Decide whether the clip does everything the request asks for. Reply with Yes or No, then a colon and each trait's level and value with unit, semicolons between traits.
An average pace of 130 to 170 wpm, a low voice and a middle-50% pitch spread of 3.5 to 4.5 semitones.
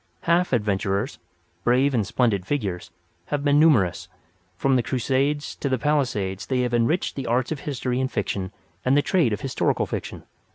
No: average, 160 wpm; low, 130 Hz; average, 5.1 semitones